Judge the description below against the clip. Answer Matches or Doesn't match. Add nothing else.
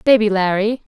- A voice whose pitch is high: Matches